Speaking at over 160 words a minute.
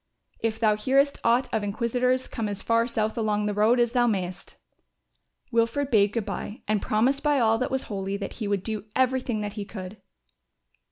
Yes: average, 190 wpm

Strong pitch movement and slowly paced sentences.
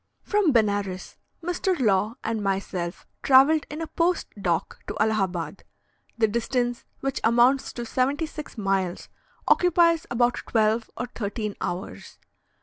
Yes: wide, 5.7 semitones; slow, 130 wpm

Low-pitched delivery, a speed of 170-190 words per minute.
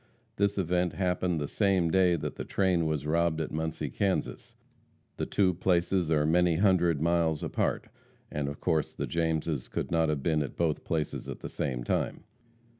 Yes: very low, 85 Hz; average, 180 wpm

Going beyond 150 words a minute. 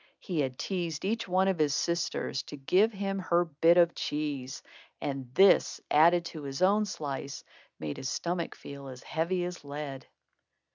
Yes: average, 170 wpm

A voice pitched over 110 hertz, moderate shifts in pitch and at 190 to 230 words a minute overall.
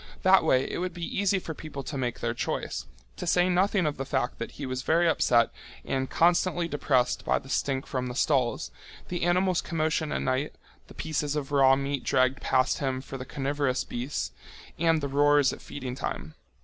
Yes: medium, 140 Hz; average, 3.9 semitones; average, 200 wpm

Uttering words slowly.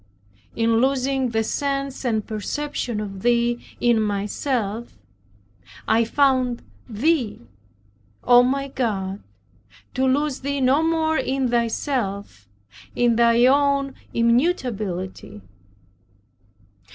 Yes: slow, 95 wpm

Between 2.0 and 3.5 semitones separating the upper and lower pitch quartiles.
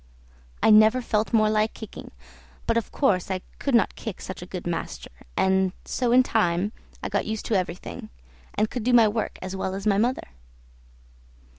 Yes: average, 3.2 semitones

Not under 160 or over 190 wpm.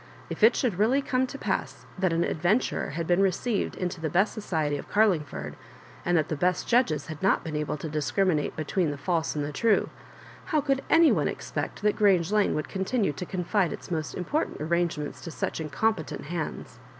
No: fast, 205 wpm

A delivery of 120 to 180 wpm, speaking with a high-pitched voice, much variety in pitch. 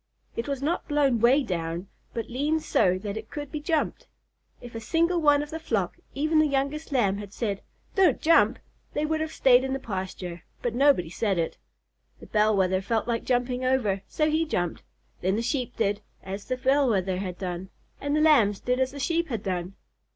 No: fast, 205 wpm; high, 245 Hz; wide, 6.8 semitones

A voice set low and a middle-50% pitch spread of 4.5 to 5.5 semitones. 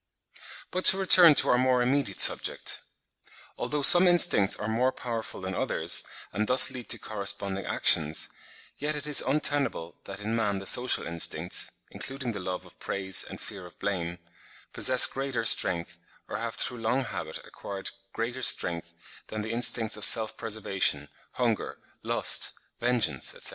Yes: low, 115 Hz; average, 5.0 semitones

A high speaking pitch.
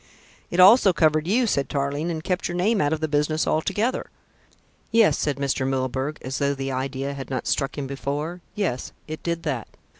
No: medium, 150 Hz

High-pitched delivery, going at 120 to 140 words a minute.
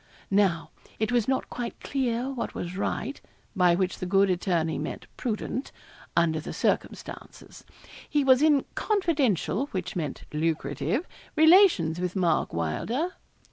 Yes: high, 195 Hz; slow, 135 wpm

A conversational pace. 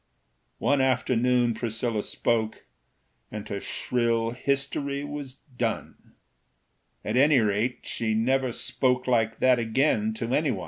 No: slow, 120 wpm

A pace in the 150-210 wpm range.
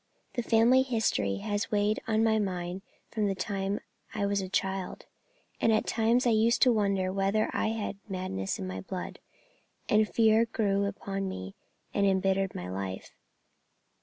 Yes: average, 165 wpm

